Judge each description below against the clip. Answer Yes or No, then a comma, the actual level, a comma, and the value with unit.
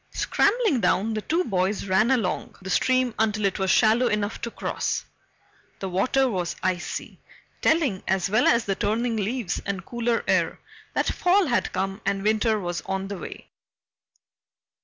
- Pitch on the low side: No, high, 215 Hz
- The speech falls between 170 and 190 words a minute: No, average, 160 wpm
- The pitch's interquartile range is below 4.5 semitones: Yes, average, 3.9 semitones